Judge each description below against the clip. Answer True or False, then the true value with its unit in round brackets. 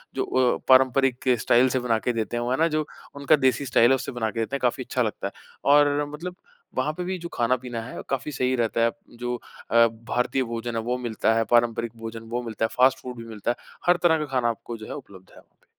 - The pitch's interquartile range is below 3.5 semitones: True (2.7 semitones)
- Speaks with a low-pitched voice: True (125 Hz)